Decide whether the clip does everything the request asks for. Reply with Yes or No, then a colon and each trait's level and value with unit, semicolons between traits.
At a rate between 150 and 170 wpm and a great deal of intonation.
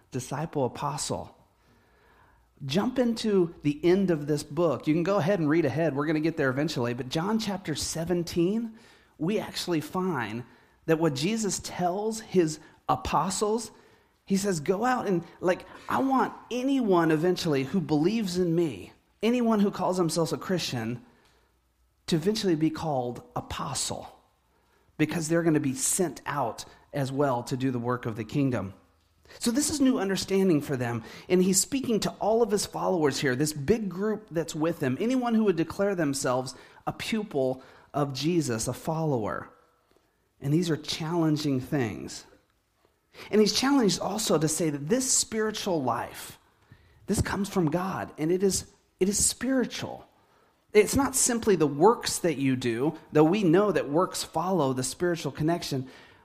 Yes: average, 160 wpm; wide, 5.7 semitones